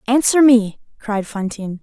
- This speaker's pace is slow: Yes, slow, 130 wpm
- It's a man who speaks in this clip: No, female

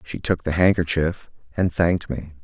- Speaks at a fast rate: No, average, 170 wpm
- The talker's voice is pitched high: No, very low, 85 Hz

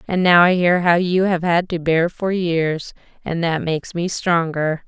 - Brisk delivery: Yes, fast, 210 wpm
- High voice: No, medium, 170 Hz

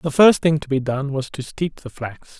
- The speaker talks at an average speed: No, fast, 275 wpm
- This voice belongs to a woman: No, male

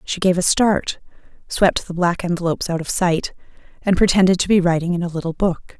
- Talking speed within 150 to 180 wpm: No, fast, 205 wpm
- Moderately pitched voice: Yes, medium, 180 Hz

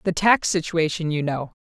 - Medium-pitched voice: Yes, medium, 165 Hz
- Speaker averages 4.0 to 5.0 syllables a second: Yes, 4.9 syllables/s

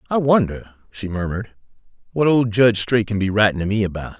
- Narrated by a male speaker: Yes, male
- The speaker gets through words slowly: No, average, 200 wpm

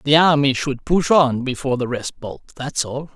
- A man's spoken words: Yes, male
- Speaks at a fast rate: Yes, fast, 210 wpm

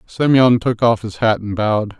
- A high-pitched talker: No, low, 115 Hz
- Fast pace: Yes, fast, 210 wpm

